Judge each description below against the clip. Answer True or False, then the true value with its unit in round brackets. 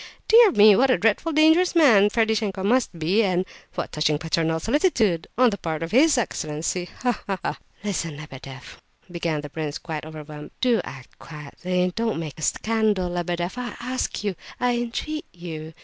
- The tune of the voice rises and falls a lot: True (6.8 semitones)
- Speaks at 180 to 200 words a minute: False (165 wpm)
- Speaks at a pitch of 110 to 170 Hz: False (185 Hz)